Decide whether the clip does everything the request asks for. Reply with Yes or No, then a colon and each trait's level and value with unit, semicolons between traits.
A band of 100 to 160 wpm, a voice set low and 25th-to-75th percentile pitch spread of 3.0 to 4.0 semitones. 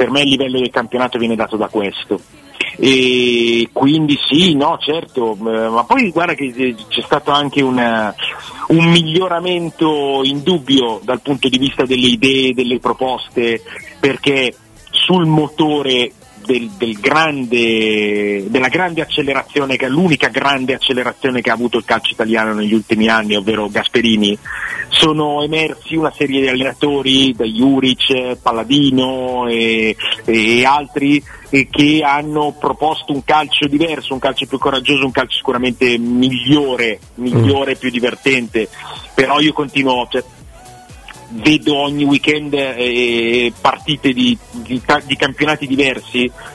Yes: average, 135 wpm; low, 130 Hz; average, 3.4 semitones